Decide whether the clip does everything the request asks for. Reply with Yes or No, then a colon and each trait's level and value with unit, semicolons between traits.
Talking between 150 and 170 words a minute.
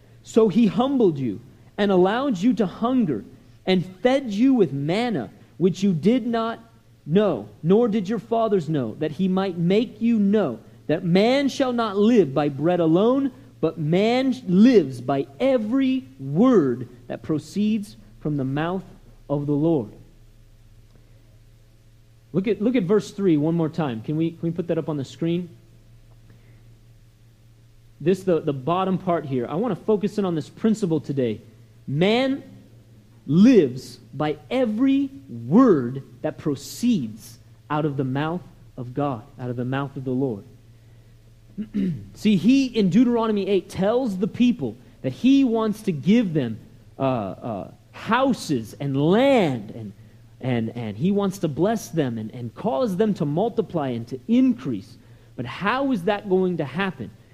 Yes: average, 155 wpm